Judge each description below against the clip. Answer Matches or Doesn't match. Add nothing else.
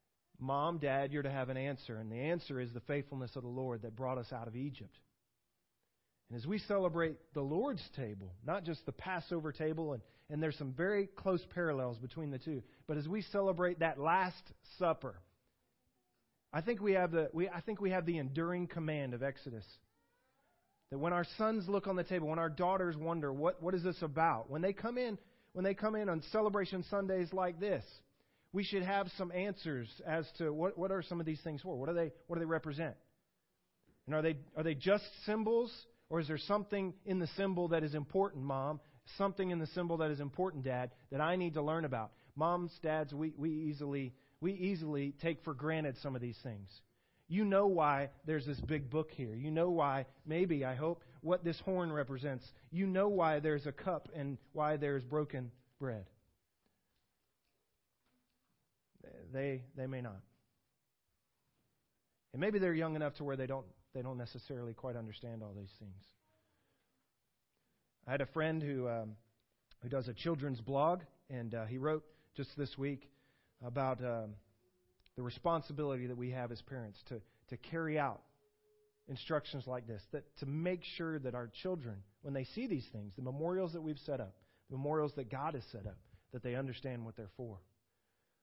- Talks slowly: Doesn't match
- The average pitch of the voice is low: Doesn't match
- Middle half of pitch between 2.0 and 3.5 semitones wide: Doesn't match